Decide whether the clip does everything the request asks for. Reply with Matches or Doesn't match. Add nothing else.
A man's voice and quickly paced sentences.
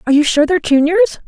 Doesn't match